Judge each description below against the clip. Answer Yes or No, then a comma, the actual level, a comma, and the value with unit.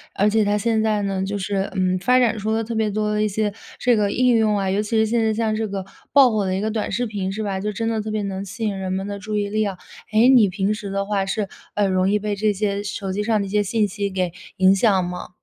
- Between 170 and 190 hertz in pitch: No, high, 210 Hz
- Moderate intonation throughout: No, narrow, 1.9 semitones